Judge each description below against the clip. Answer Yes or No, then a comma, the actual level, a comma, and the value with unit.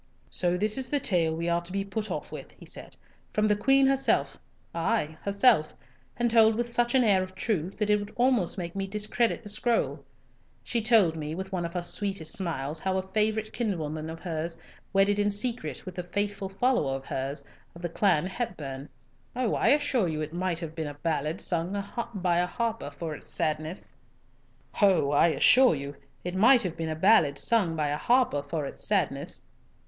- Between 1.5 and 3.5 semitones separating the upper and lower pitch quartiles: No, average, 4.7 semitones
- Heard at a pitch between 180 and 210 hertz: Yes, high, 190 Hz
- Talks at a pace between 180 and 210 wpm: No, average, 165 wpm